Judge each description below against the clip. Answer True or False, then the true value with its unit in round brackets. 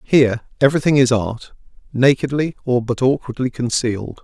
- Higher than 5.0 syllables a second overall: True (5.5 syllables/s)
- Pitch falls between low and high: False (125 Hz)